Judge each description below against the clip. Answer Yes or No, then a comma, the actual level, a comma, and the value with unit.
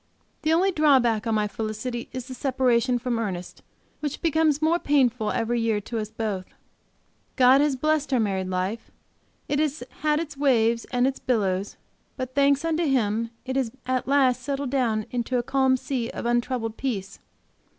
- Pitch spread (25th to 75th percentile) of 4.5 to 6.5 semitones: No, average, 3.7 semitones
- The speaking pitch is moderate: No, very high, 250 Hz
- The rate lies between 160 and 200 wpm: Yes, average, 170 wpm